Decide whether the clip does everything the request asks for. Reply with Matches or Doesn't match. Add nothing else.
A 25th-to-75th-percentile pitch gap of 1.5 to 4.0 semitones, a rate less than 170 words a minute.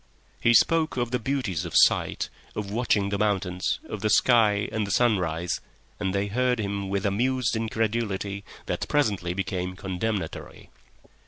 Matches